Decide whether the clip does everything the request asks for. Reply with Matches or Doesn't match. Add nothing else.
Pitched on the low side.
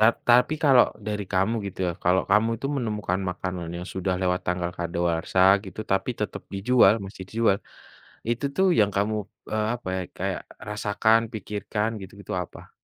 Matches